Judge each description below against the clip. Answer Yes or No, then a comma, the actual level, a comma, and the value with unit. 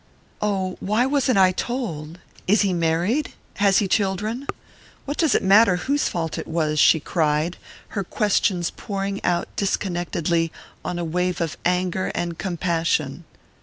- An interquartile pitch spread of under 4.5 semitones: Yes, average, 3.4 semitones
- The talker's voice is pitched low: No, medium, 185 Hz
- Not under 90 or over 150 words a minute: Yes, average, 145 wpm